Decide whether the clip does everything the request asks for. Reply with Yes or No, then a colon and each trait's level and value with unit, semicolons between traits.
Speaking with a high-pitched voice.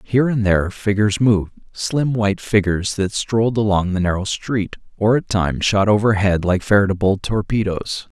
No: low, 105 Hz